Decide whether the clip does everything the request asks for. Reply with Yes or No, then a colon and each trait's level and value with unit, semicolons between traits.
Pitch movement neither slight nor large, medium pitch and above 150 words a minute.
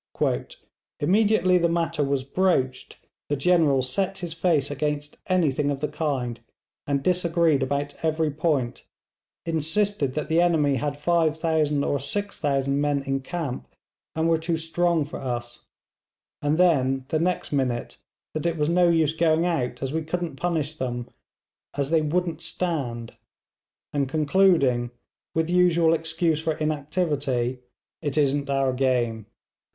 No: average, 3.5 semitones; medium, 155 Hz; average, 140 wpm